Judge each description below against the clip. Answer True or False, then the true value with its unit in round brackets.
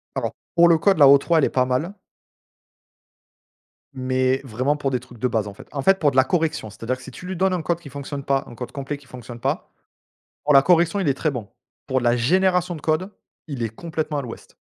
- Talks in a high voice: False (140 Hz)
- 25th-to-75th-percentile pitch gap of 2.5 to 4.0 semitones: False (4.5 semitones)